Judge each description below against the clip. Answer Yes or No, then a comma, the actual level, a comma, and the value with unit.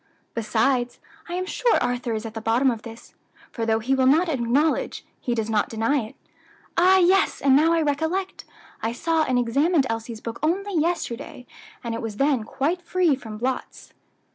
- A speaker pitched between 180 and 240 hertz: No, very high, 260 Hz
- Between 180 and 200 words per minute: Yes, average, 185 wpm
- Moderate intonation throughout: No, wide, 6.0 semitones